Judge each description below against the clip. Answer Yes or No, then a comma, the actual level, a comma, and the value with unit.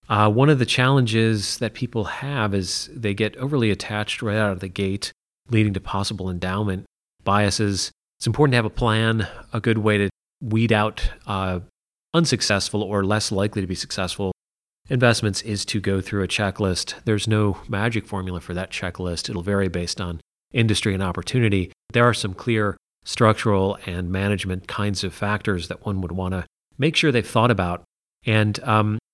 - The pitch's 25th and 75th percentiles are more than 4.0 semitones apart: No, average, 2.8 semitones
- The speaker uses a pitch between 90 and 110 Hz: Yes, low, 105 Hz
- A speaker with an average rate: Yes, average, 175 wpm